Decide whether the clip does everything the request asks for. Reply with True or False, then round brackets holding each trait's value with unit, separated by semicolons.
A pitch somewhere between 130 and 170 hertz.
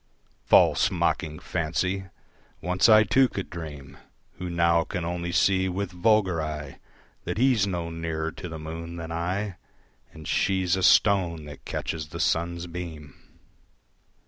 False (85 Hz)